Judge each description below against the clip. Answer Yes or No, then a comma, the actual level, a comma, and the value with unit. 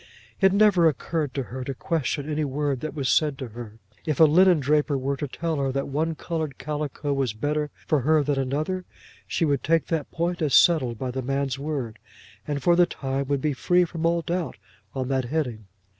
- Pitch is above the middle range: No, medium, 145 Hz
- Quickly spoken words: Yes, fast, 210 wpm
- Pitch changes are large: No, average, 3.2 semitones